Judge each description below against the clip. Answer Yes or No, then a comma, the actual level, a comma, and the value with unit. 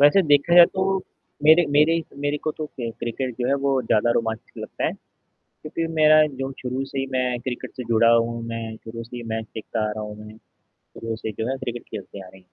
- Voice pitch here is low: Yes, low, 125 Hz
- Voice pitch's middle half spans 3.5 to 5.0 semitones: Yes, average, 4.3 semitones